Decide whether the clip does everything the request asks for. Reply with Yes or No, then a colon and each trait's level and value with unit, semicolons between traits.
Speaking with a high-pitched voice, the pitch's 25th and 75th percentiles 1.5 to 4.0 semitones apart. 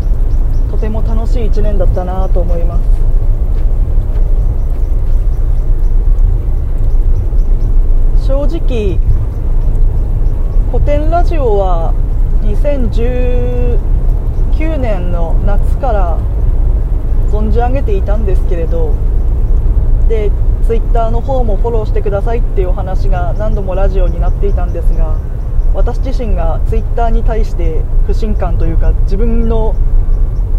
No: low, 105 Hz; average, 2.9 semitones